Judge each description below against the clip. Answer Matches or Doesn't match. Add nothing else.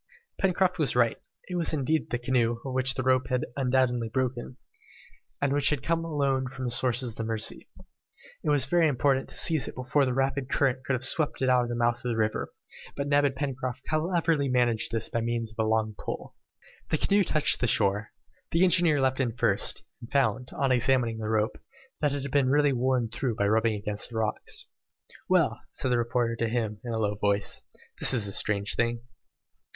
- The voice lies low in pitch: Matches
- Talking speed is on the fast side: Matches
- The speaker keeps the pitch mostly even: Doesn't match